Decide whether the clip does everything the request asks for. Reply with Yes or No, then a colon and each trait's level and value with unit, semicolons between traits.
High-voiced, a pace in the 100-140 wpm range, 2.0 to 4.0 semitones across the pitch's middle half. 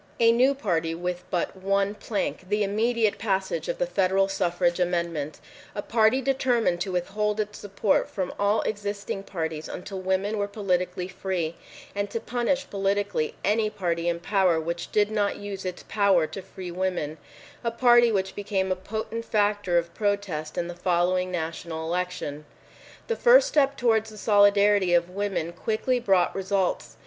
No: high, 195 Hz; average, 155 wpm; average, 3.0 semitones